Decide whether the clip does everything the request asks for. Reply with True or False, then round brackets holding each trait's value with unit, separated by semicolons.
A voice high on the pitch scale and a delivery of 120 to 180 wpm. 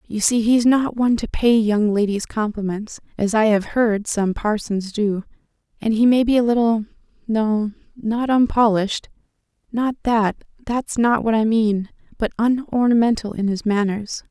True (220 Hz; 145 wpm)